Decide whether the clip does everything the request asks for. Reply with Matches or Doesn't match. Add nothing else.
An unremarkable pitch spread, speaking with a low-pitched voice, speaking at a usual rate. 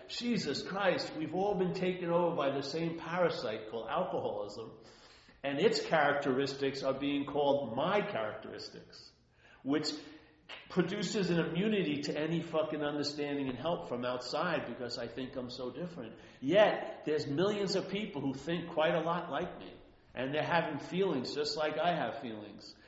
Doesn't match